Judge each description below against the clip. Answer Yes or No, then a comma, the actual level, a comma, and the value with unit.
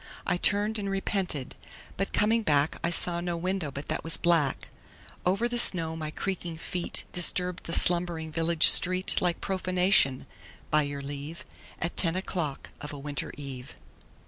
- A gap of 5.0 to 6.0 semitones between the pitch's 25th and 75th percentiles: No, average, 3.5 semitones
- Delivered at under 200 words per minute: Yes, average, 160 wpm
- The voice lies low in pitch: No, medium, 170 Hz